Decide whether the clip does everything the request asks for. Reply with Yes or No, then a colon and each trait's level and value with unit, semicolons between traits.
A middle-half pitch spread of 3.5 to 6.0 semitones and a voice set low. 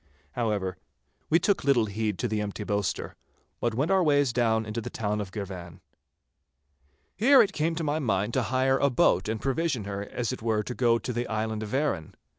Yes: average, 4.6 semitones; low, 115 Hz